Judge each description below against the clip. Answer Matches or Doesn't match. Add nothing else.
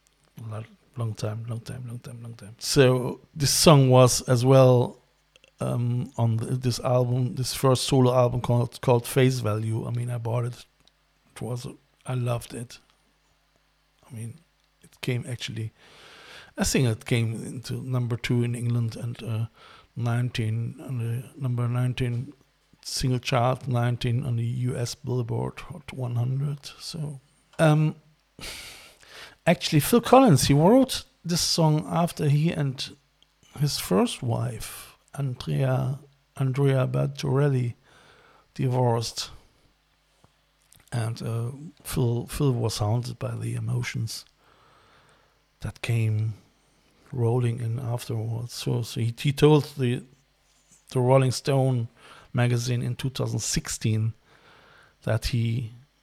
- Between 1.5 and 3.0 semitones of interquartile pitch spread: Matches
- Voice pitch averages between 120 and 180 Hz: Matches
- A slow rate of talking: Matches